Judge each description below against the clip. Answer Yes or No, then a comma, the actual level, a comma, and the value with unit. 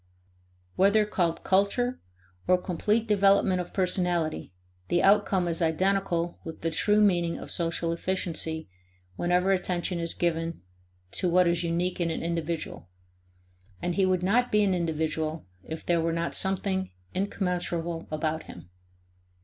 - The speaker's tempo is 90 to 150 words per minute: Yes, average, 140 wpm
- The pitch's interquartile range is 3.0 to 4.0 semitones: No, narrow, 2.5 semitones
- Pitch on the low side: No, medium, 175 Hz